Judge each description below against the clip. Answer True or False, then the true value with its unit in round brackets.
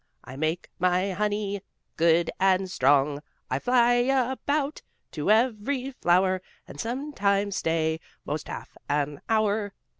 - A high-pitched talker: True (195 Hz)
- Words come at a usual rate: False (120 wpm)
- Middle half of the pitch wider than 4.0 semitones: True (5.3 semitones)